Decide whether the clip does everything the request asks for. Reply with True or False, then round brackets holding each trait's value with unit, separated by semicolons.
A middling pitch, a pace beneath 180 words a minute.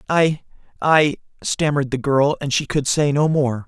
True (145 Hz; 165 wpm)